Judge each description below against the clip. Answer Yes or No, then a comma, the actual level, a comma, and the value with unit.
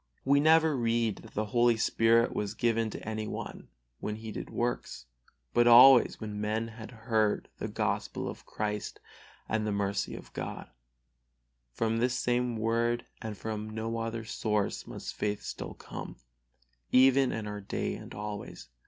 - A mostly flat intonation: Yes, narrow, 1.9 semitones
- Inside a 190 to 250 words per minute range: No, average, 160 wpm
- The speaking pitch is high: No, low, 110 Hz